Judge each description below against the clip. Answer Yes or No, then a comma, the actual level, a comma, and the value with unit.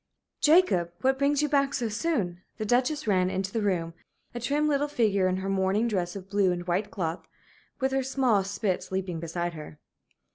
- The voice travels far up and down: Yes, wide, 6.5 semitones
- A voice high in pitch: Yes, high, 200 Hz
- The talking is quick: No, average, 195 wpm